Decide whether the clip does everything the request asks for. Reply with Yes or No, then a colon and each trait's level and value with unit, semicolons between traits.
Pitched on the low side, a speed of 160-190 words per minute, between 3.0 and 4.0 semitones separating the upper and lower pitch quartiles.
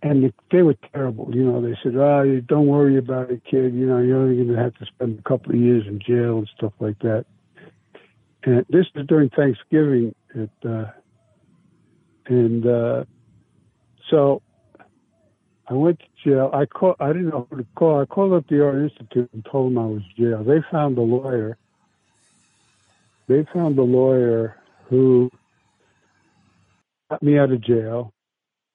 Yes: low, 130 Hz; average, 175 wpm; average, 3.3 semitones